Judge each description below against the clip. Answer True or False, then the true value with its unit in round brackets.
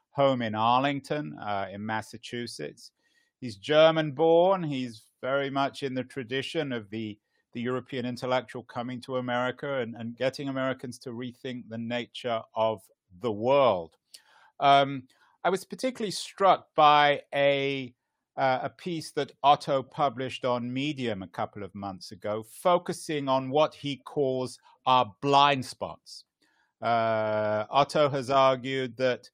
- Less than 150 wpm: True (135 wpm)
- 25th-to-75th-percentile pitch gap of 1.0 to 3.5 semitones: True (3.1 semitones)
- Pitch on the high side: False (130 Hz)